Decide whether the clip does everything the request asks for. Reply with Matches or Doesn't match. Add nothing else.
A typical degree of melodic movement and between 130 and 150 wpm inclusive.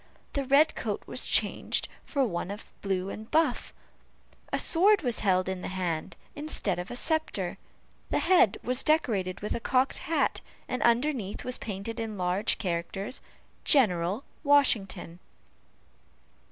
Doesn't match